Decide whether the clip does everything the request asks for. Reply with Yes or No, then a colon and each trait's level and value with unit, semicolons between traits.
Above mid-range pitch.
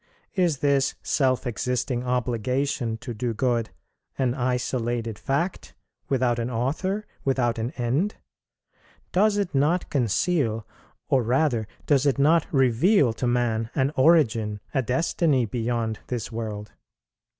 No: low, 125 Hz